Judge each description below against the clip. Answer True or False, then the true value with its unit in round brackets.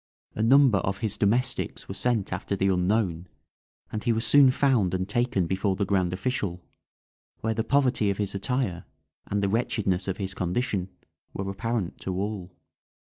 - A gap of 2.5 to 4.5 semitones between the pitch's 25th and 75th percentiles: True (3.6 semitones)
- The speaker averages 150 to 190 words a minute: True (170 wpm)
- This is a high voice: False (100 Hz)